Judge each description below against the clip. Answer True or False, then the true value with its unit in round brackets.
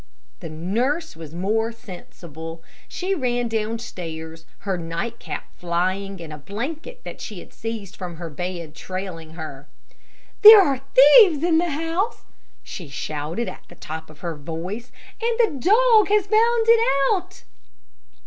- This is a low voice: False (200 Hz)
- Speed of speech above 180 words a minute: False (150 wpm)